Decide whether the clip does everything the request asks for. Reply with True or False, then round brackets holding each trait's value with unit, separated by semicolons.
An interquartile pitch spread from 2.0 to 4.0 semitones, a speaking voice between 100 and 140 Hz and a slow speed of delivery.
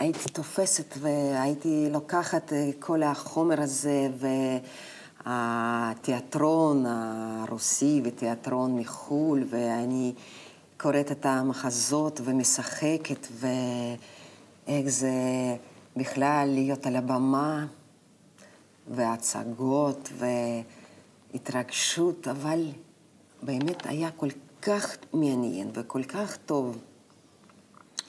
True (3.1 semitones; 135 Hz; 70 wpm)